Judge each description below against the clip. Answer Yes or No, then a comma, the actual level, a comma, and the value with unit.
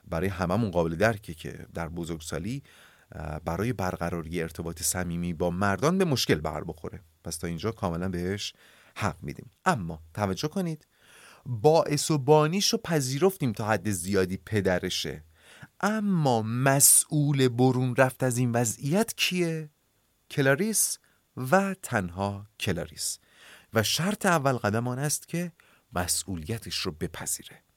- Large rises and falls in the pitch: Yes, wide, 8.5 semitones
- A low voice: Yes, low, 115 Hz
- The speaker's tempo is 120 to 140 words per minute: Yes, average, 125 wpm